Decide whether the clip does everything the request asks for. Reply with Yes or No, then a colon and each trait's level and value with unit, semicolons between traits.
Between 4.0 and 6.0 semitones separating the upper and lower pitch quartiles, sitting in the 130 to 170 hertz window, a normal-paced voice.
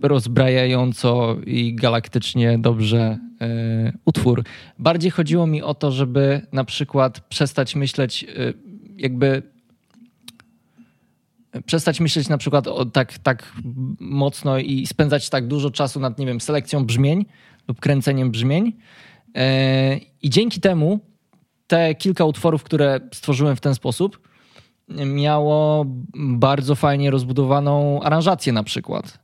No: average, 3.2 semitones; medium, 140 Hz; average, 120 wpm